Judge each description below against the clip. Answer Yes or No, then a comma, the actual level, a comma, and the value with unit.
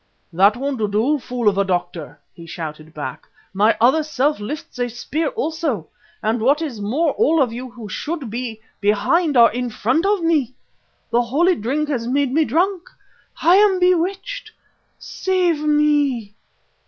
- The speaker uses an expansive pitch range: Yes, wide, 6.6 semitones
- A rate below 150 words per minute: No, average, 160 wpm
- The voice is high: Yes, very high, 260 Hz